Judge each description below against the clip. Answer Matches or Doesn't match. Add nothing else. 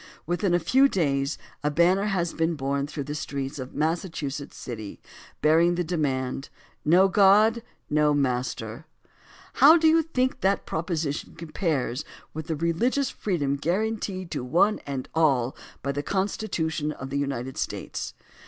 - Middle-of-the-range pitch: Matches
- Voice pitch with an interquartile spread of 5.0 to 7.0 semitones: Matches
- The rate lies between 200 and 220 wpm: Doesn't match